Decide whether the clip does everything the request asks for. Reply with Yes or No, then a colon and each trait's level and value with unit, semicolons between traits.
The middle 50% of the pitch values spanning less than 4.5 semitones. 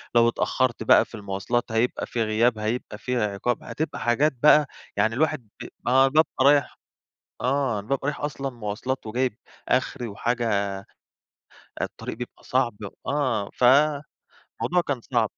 Yes: average, 3.5 semitones